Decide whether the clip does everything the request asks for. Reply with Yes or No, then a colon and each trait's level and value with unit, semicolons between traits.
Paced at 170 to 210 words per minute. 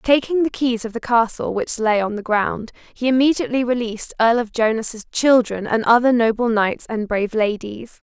Yes: average, 185 wpm